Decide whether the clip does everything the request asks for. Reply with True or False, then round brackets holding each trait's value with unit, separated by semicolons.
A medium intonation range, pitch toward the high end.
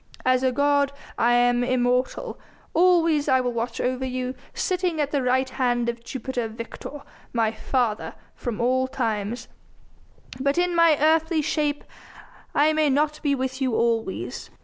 True (3.4 semitones; 260 Hz)